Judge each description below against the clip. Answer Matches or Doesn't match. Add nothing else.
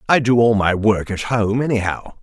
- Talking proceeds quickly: Matches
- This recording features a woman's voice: Doesn't match